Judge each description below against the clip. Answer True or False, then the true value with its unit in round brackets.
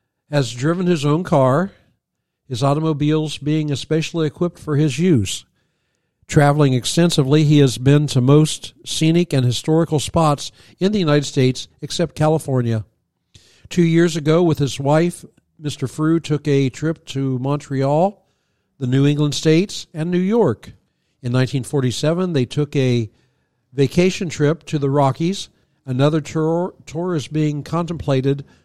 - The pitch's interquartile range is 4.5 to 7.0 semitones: False (3.2 semitones)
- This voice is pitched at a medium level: True (150 Hz)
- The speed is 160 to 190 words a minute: False (140 wpm)